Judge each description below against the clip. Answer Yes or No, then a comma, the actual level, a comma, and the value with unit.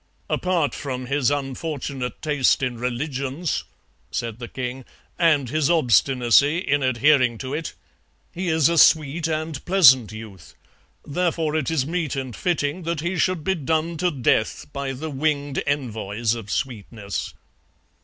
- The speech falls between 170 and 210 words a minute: No, average, 145 wpm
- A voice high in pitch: No, medium, 140 Hz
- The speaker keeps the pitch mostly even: No, average, 4.0 semitones